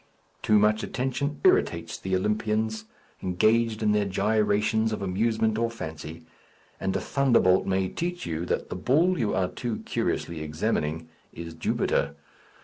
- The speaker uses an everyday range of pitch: Yes, average, 3.8 semitones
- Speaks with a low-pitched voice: Yes, low, 105 Hz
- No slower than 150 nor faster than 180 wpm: No, average, 140 wpm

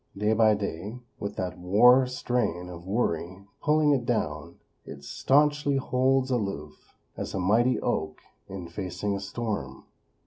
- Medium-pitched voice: No, low, 105 Hz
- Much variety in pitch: Yes, wide, 5.9 semitones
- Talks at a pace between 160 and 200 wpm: No, average, 140 wpm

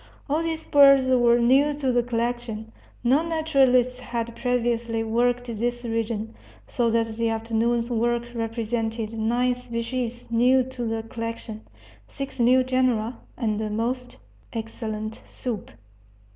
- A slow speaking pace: Yes, slow, 130 wpm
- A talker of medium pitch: No, high, 235 Hz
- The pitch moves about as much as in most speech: No, narrow, 1.8 semitones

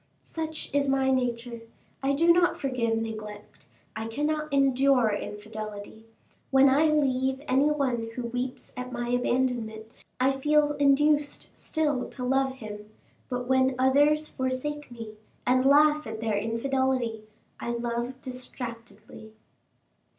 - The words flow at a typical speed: No, slow, 130 wpm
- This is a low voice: No, very high, 255 Hz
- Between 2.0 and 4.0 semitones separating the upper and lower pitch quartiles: Yes, average, 3.2 semitones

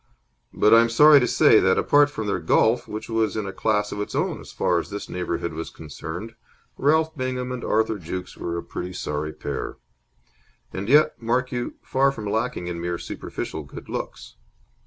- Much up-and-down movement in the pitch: Yes, wide, 5.9 semitones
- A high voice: No, low, 110 Hz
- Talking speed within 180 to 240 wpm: Yes, average, 190 wpm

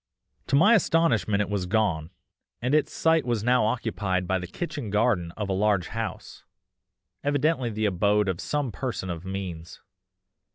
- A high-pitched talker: No, low, 105 Hz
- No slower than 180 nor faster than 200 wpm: No, average, 160 wpm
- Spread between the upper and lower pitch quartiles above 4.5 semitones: Yes, average, 5.0 semitones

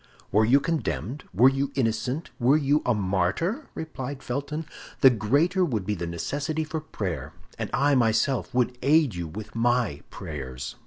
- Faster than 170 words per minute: No, average, 160 wpm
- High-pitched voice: No, low, 125 Hz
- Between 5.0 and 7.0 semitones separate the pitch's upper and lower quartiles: Yes, wide, 5.4 semitones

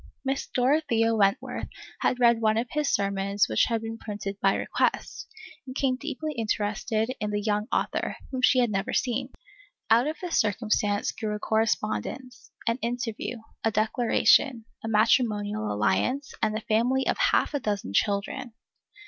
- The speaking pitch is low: No, high, 225 Hz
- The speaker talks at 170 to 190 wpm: No, average, 155 wpm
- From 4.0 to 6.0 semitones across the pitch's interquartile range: No, average, 3.3 semitones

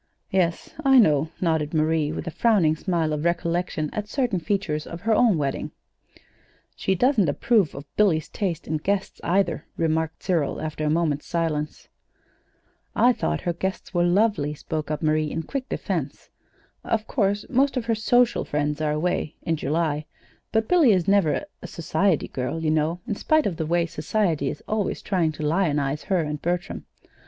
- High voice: No, medium, 170 Hz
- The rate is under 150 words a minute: No, average, 175 wpm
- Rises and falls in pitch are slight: No, average, 4.6 semitones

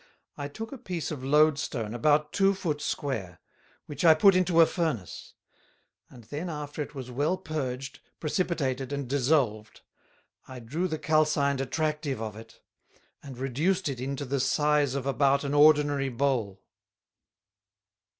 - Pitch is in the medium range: Yes, medium, 145 Hz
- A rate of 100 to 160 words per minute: Yes, average, 150 wpm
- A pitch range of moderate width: Yes, average, 3.1 semitones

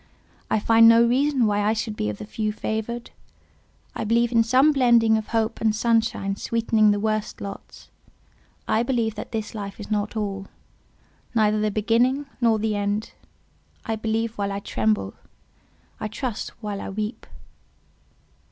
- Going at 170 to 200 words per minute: No, average, 160 wpm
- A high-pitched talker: Yes, high, 220 Hz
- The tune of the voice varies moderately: No, narrow, 1.8 semitones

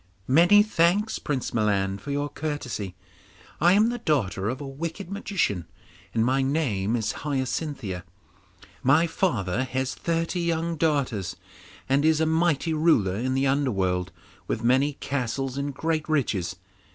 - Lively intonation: Yes, wide, 6.2 semitones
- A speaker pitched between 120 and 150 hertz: Yes, medium, 140 Hz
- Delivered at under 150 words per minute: Yes, average, 140 wpm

